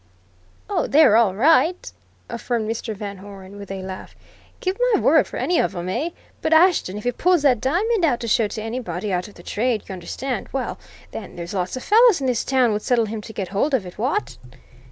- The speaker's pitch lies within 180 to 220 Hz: No, high, 230 Hz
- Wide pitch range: Yes, wide, 5.9 semitones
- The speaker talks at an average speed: No, fast, 220 wpm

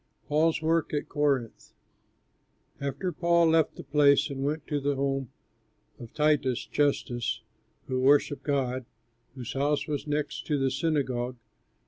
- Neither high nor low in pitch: Yes, medium, 145 Hz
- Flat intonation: Yes, narrow, 2.2 semitones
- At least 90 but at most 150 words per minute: Yes, slow, 135 wpm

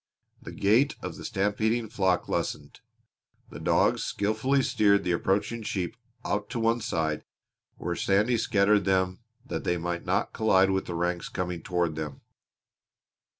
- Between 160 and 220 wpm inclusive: No, average, 150 wpm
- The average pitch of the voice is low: Yes, low, 100 Hz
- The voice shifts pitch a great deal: No, average, 3.7 semitones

